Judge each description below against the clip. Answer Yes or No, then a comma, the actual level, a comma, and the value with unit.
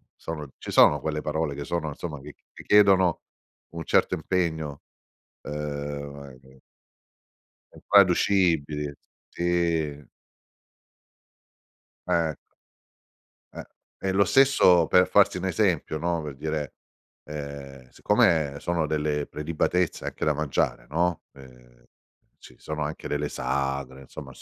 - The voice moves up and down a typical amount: Yes, average, 3.2 semitones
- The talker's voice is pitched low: Yes, very low, 75 Hz